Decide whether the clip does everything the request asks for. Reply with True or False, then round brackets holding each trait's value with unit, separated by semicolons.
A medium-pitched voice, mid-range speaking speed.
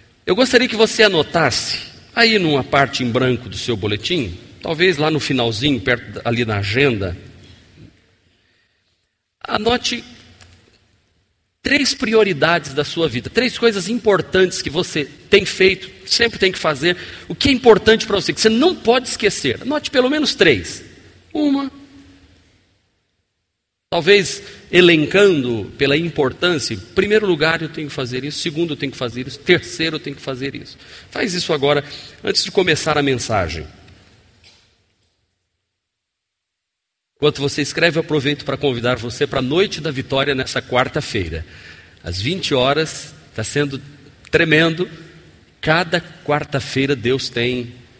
True (145 Hz; 140 wpm)